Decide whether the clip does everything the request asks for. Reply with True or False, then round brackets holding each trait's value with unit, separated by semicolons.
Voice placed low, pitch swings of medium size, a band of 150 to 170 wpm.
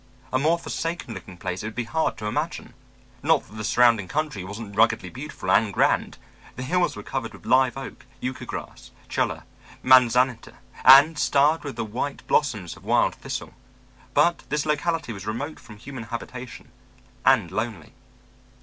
True (125 Hz; 5.0 semitones; 165 wpm)